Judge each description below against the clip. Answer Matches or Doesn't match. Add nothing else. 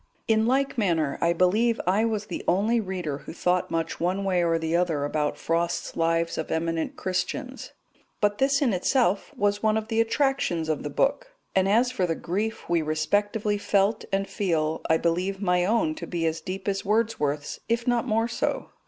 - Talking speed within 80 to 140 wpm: Doesn't match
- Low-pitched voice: Doesn't match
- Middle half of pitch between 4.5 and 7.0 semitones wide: Matches